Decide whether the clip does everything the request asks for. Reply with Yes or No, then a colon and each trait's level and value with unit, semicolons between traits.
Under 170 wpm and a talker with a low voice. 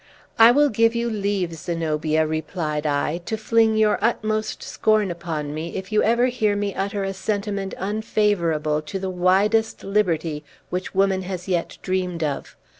No: average, 160 wpm; high, 195 Hz